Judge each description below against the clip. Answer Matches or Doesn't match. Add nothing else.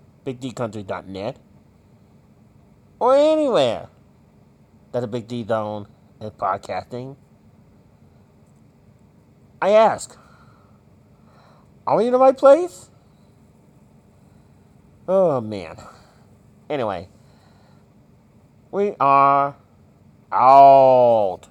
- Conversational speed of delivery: Doesn't match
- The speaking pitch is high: Doesn't match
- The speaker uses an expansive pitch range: Matches